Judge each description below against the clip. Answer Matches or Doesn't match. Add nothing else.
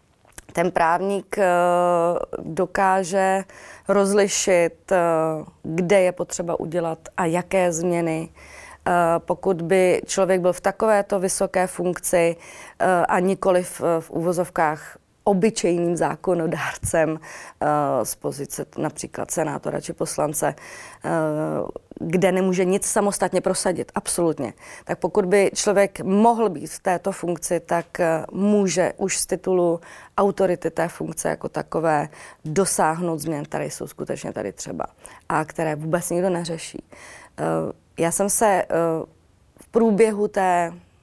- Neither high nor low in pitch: Matches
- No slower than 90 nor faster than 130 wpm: Matches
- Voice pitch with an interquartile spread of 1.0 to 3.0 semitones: Matches